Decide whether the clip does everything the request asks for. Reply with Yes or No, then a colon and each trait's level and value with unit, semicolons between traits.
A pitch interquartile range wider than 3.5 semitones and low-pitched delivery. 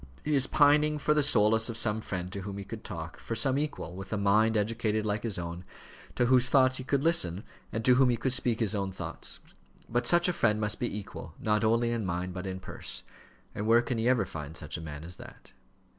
Yes: average, 4.6 semitones; low, 110 Hz